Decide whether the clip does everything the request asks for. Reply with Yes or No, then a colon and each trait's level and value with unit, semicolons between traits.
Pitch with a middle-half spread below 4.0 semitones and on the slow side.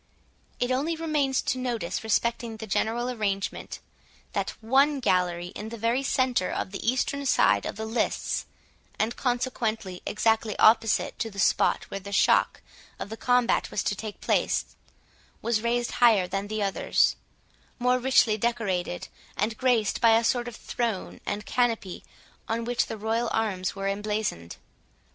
No: average, 3.0 semitones; average, 155 wpm